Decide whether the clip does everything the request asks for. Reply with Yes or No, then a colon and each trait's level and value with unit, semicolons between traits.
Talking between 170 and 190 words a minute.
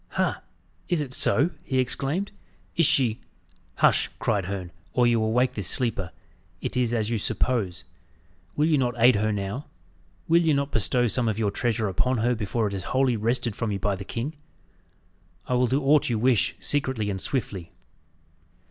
Yes: average, 185 wpm